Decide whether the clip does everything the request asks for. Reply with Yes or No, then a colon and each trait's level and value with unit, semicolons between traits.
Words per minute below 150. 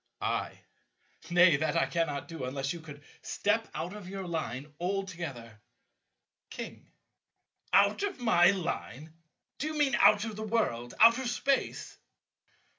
Yes: average, 140 wpm